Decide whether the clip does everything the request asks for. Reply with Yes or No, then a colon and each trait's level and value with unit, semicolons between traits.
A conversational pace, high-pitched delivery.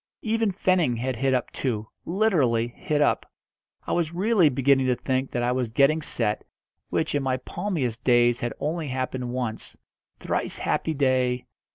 No: average, 165 wpm; low, 130 Hz